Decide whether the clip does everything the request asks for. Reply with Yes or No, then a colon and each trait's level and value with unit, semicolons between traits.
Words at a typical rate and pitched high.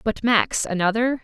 Yes: average, 145 wpm; high, 225 Hz